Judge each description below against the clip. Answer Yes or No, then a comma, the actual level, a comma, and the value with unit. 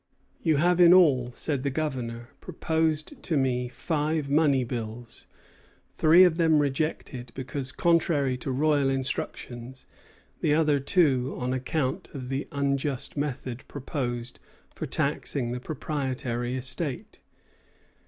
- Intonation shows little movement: No, average, 3.4 semitones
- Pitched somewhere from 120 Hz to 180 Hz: Yes, medium, 140 Hz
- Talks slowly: Yes, slow, 125 wpm